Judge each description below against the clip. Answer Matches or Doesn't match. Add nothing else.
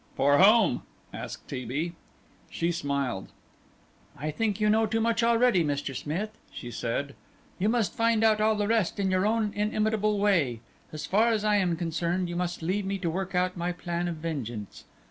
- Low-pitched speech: Doesn't match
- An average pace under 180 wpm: Doesn't match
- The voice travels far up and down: Doesn't match